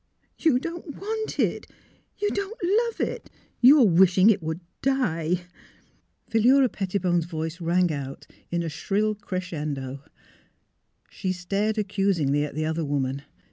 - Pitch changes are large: Yes, wide, 5.9 semitones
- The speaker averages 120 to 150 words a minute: Yes, average, 145 wpm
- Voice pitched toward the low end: No, medium, 185 Hz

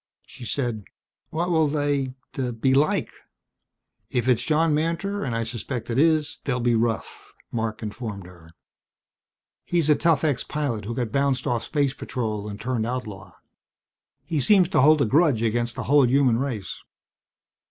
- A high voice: No, low, 130 Hz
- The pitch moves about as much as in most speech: Yes, average, 4.5 semitones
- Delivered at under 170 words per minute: Yes, average, 160 wpm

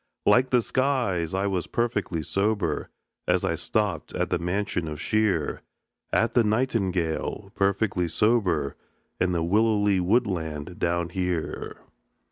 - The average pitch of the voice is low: Yes, very low, 95 Hz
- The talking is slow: Yes, slow, 125 wpm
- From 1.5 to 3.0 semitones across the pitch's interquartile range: No, average, 4.1 semitones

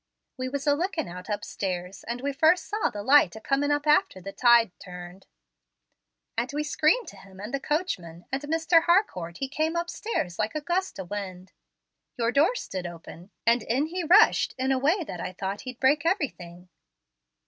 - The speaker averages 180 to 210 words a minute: Yes, average, 190 wpm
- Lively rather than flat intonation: Yes, wide, 8.5 semitones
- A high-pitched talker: Yes, very high, 260 Hz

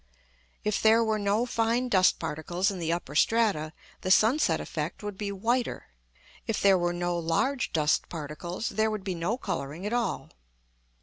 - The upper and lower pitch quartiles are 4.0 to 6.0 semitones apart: Yes, average, 4.5 semitones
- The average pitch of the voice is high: Yes, high, 200 Hz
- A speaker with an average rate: Yes, average, 170 wpm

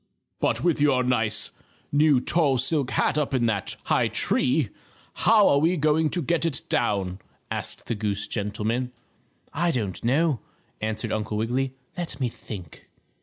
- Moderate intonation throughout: No, wide, 5.7 semitones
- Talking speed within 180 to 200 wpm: No, average, 160 wpm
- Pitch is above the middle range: No, low, 130 Hz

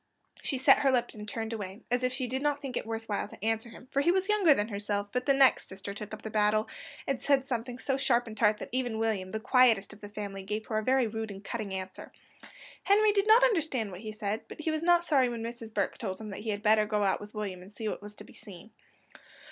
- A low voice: No, high, 225 Hz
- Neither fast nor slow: No, fast, 275 wpm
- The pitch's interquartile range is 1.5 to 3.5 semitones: No, average, 4.0 semitones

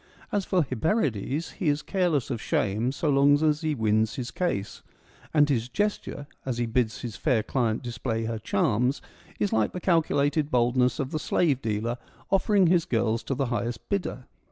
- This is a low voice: Yes, low, 130 Hz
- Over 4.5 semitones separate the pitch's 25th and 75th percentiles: Yes, average, 5.3 semitones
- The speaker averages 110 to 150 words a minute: No, average, 180 wpm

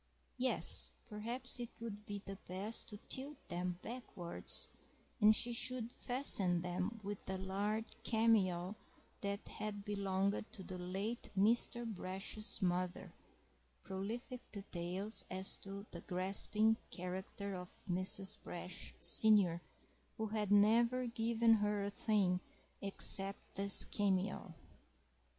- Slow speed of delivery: Yes, slow, 120 wpm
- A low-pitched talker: No, high, 200 Hz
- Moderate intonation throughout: Yes, average, 3.0 semitones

